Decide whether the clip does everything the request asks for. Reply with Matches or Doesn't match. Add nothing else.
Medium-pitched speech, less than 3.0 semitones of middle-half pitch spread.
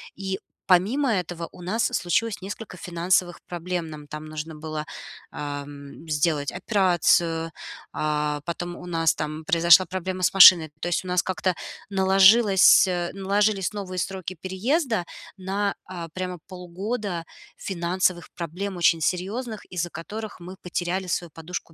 Matches